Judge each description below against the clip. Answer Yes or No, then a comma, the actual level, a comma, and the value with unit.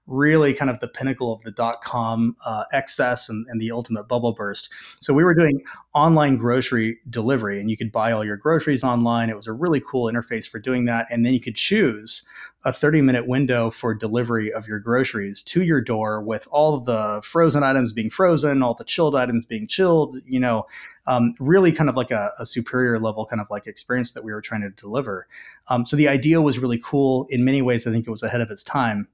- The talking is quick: Yes, fast, 230 wpm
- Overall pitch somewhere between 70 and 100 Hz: No, low, 120 Hz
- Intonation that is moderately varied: Yes, average, 3.5 semitones